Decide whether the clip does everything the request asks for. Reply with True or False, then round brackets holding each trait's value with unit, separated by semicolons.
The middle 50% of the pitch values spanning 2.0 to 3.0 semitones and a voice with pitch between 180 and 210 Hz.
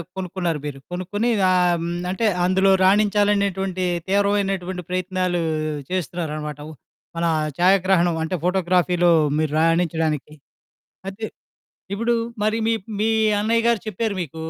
True (2.6 semitones; 185 Hz)